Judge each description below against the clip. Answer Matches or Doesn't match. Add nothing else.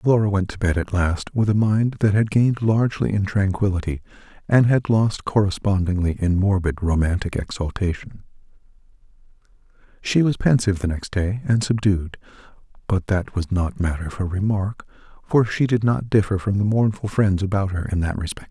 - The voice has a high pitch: Doesn't match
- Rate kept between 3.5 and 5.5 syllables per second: Matches